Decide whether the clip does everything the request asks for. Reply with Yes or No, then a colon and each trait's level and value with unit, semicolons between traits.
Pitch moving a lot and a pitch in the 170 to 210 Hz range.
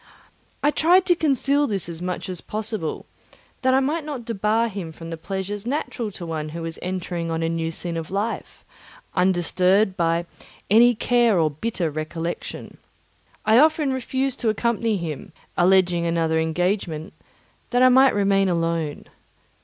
Yes: wide, 6.1 semitones; high, 190 Hz